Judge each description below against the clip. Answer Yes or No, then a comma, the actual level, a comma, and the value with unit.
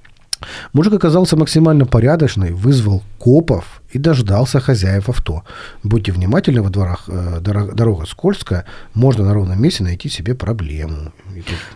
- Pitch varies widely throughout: Yes, wide, 6.1 semitones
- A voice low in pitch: Yes, low, 105 Hz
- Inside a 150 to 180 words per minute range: No, average, 115 wpm